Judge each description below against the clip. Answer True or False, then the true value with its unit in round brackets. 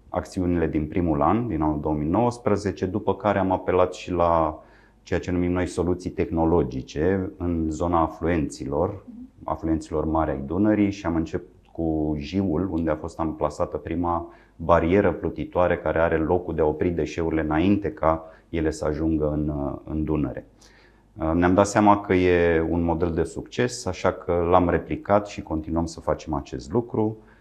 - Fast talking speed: False (160 wpm)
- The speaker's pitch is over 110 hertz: False (85 Hz)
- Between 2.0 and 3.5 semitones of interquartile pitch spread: True (3.2 semitones)